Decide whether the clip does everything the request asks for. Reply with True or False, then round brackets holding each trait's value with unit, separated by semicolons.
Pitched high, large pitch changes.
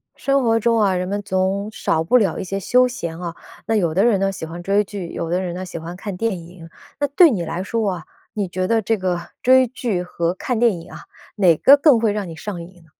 False (195 Hz; 4.3 semitones)